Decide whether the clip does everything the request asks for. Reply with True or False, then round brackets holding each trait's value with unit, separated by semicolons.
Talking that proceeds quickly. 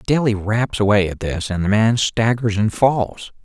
False (190 wpm)